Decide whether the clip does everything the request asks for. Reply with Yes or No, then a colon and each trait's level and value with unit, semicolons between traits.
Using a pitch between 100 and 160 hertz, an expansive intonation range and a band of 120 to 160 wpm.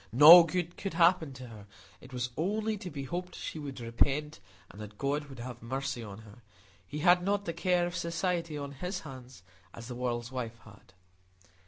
No: medium, 140 Hz; wide, 6.2 semitones; average, 195 wpm